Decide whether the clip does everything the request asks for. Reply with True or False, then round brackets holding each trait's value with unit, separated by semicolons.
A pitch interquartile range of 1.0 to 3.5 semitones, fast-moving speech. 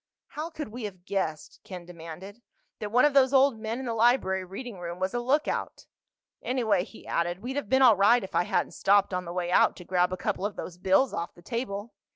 False (5.2 semitones; 230 wpm)